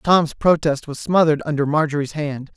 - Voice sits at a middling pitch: Yes, medium, 150 Hz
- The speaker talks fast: No, average, 165 wpm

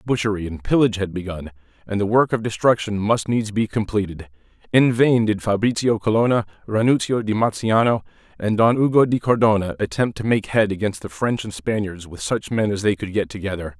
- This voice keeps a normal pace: Yes, average, 190 wpm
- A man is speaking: Yes, male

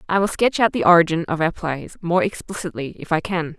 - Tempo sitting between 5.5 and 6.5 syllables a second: Yes, 5.6 syllables/s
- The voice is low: No, medium, 175 Hz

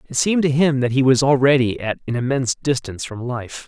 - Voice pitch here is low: Yes, low, 130 Hz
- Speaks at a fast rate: Yes, fast, 230 wpm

